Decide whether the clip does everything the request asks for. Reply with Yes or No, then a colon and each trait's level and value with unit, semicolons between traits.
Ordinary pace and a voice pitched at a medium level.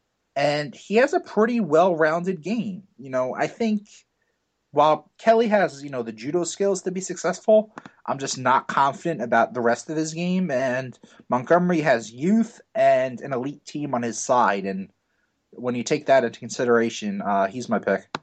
Yes: average, 180 wpm; medium, 165 Hz